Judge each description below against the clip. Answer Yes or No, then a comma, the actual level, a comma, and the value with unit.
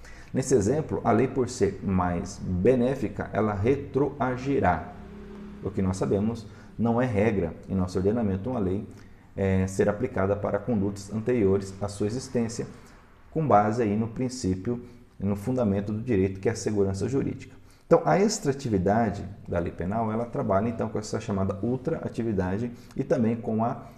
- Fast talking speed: No, average, 155 wpm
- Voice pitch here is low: Yes, low, 105 Hz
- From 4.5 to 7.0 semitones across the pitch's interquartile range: No, average, 3.7 semitones